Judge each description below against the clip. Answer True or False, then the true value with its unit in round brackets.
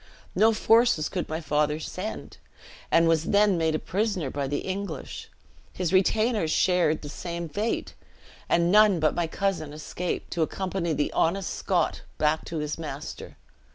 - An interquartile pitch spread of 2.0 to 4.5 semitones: True (3.9 semitones)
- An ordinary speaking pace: True (155 wpm)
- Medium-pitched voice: True (170 Hz)